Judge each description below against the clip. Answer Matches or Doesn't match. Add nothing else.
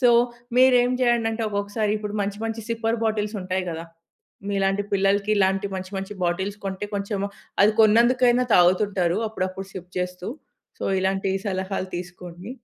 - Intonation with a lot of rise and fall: Doesn't match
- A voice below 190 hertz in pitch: Doesn't match